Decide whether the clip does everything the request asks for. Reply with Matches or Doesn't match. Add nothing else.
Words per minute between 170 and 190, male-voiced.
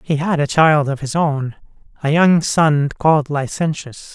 Matches